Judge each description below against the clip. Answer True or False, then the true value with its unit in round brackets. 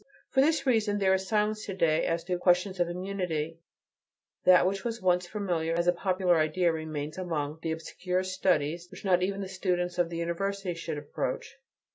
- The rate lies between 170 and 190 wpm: True (185 wpm)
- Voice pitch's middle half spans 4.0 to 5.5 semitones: False (2.6 semitones)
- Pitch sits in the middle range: True (180 Hz)